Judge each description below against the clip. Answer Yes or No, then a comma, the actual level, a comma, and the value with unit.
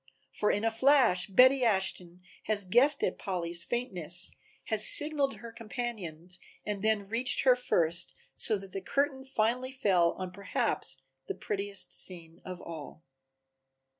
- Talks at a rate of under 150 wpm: Yes, average, 140 wpm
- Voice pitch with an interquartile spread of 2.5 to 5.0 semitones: No, wide, 5.5 semitones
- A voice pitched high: Yes, high, 205 Hz